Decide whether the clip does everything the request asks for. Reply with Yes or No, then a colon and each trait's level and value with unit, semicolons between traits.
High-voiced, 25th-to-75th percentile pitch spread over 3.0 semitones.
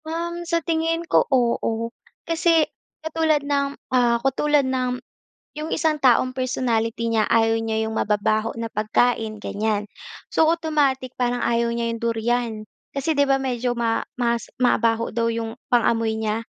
Yes: high, 245 Hz; average, 3.9 semitones